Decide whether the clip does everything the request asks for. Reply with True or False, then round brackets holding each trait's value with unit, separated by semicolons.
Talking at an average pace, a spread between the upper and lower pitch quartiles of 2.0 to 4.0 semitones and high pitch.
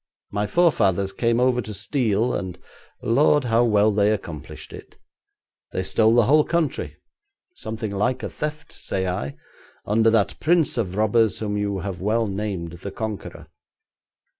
False (150 wpm; 3.3 semitones; 110 Hz)